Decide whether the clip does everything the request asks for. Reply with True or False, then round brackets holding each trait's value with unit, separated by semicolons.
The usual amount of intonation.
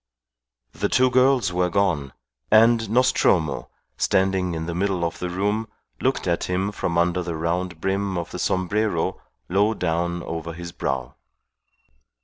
True (3.1 semitones)